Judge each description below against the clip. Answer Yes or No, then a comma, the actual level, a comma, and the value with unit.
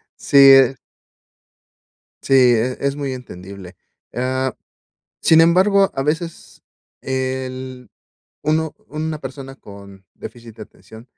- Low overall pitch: Yes, low, 130 Hz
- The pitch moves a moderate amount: Yes, average, 3.5 semitones